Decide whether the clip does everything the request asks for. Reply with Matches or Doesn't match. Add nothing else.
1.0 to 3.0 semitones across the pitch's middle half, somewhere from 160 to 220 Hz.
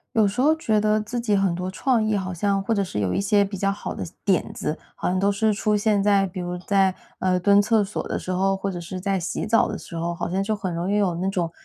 Matches